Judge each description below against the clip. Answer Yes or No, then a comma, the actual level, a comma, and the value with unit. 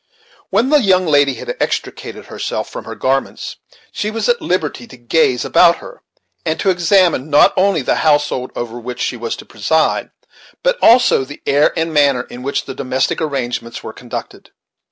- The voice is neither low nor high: Yes, medium, 145 Hz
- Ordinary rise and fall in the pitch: No, wide, 6.4 semitones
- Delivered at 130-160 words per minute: No, average, 175 wpm